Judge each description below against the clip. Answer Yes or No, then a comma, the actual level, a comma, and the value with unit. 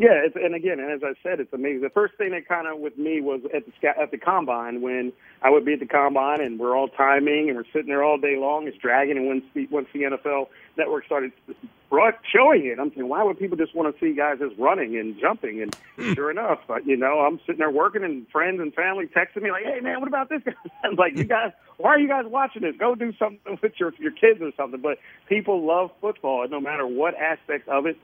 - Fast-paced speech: Yes, fast, 255 wpm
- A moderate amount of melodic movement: No, wide, 6.4 semitones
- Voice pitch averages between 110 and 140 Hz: No, medium, 155 Hz